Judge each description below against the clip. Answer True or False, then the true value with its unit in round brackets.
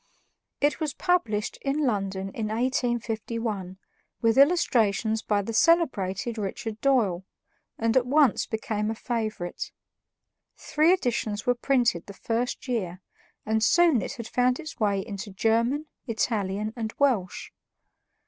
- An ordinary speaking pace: False (130 wpm)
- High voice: True (225 Hz)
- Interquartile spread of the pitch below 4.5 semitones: True (3.6 semitones)